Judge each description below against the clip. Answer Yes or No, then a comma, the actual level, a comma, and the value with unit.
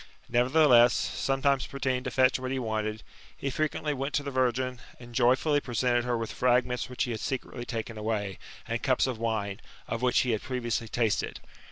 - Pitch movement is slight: Yes, narrow, 2.2 semitones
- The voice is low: Yes, low, 125 Hz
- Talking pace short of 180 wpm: No, average, 185 wpm